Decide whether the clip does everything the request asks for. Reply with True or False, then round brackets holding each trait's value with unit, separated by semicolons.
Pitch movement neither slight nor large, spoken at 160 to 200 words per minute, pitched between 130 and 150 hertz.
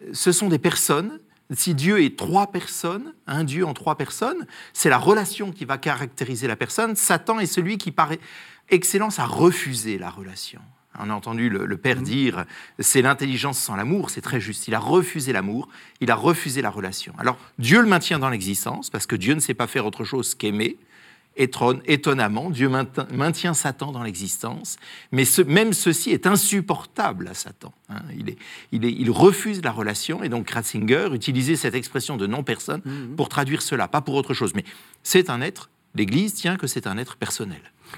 False (6.3 semitones; 195 wpm; 140 Hz)